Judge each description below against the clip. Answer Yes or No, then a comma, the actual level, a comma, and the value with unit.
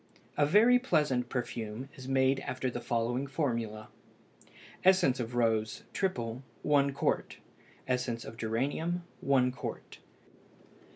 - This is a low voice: Yes, low, 130 Hz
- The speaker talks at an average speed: No, slow, 115 wpm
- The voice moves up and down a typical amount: Yes, average, 3.2 semitones